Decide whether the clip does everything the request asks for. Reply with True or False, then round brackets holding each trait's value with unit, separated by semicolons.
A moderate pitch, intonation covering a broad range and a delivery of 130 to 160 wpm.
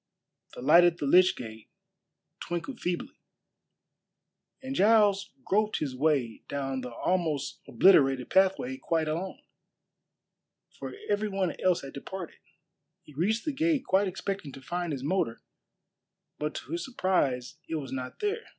True (175 Hz; 6.2 semitones; 140 wpm)